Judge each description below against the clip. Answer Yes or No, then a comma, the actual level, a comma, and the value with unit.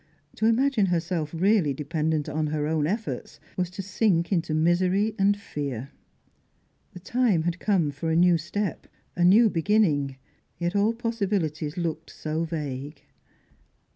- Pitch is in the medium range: Yes, medium, 170 Hz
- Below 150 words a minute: Yes, average, 140 wpm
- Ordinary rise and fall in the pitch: Yes, average, 4.6 semitones